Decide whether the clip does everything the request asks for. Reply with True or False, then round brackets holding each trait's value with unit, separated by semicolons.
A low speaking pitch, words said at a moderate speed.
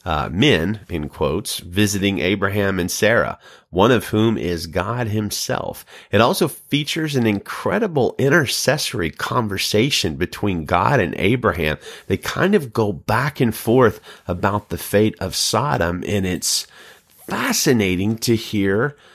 False (105 Hz; 130 wpm)